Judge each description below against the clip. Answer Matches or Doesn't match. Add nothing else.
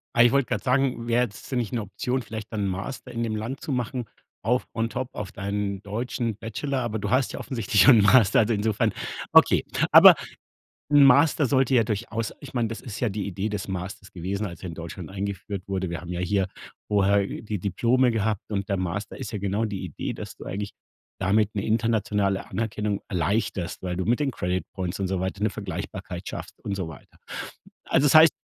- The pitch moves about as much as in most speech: Matches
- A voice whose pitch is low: Matches